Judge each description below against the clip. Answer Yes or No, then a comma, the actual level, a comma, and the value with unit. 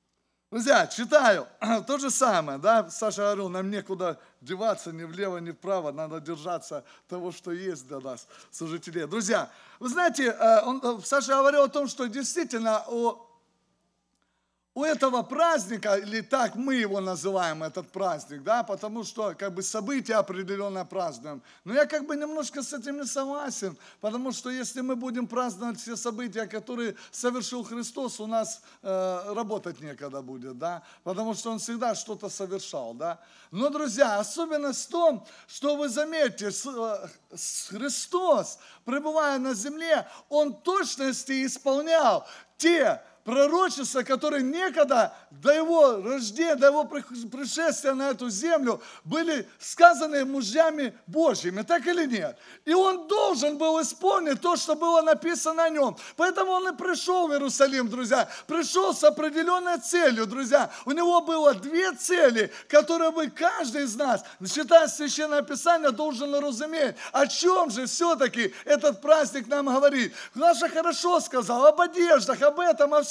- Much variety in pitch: Yes, wide, 5.9 semitones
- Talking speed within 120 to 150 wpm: Yes, average, 145 wpm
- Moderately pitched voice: No, very high, 270 Hz